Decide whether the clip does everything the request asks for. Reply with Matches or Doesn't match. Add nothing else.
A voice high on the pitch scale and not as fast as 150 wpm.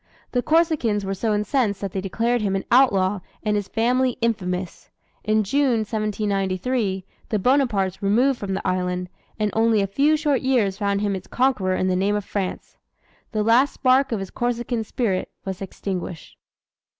Doesn't match